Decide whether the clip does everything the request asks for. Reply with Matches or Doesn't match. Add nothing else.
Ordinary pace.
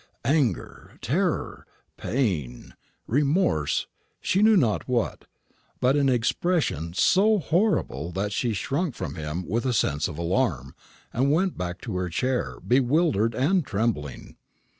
Doesn't match